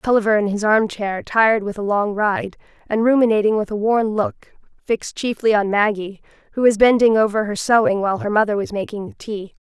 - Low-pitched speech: No, high, 210 Hz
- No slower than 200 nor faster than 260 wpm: Yes, fast, 205 wpm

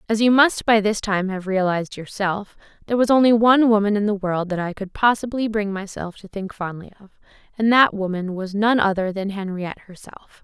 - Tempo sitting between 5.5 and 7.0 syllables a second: Yes, 5.7 syllables/s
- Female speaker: Yes, female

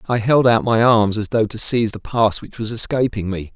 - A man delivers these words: Yes, male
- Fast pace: Yes, fast, 255 wpm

